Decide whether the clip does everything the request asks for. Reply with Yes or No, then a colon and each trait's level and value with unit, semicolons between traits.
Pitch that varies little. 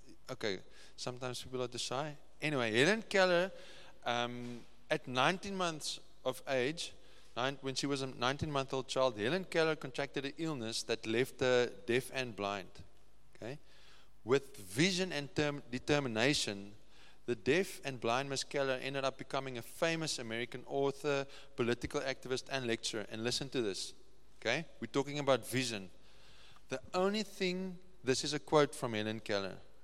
No: average, 3.8 semitones